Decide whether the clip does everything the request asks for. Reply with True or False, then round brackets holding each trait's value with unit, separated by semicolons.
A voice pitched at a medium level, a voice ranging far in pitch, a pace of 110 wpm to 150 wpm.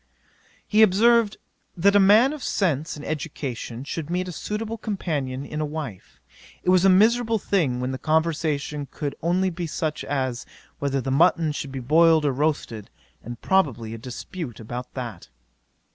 False (155 Hz; 5.9 semitones; 165 wpm)